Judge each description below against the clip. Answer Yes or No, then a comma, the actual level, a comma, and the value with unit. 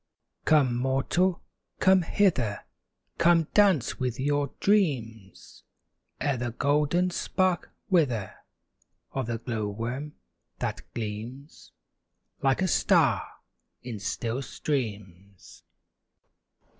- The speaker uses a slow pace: Yes, slow, 95 wpm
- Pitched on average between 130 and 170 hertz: Yes, low, 135 Hz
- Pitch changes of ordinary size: No, wide, 6.3 semitones